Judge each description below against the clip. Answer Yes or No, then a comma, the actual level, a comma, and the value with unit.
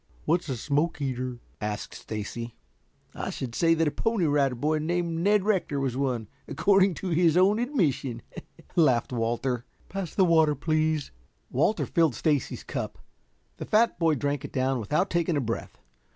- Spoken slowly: No, average, 165 wpm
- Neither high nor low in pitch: Yes, medium, 150 Hz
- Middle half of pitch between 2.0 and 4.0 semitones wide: No, average, 5.1 semitones